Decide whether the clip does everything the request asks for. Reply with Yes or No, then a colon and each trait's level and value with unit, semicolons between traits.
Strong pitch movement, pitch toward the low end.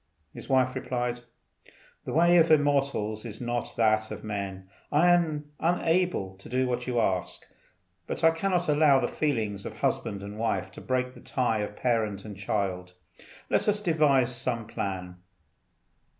Yes: wide, 6.1 semitones; low, 120 Hz